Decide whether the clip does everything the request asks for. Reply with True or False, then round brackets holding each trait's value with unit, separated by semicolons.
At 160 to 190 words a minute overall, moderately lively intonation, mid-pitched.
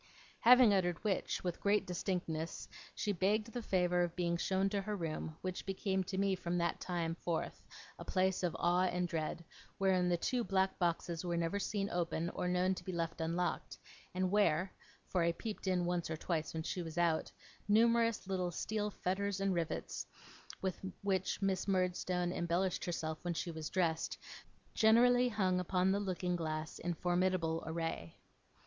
False (175 wpm; 2.3 semitones; 180 Hz)